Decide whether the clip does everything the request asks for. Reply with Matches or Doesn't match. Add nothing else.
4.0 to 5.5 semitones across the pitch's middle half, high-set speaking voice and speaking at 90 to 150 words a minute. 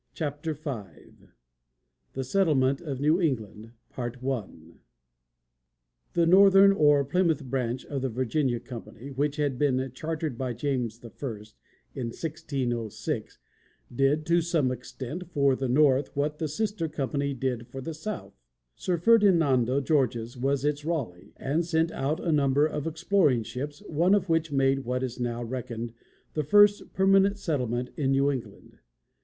Doesn't match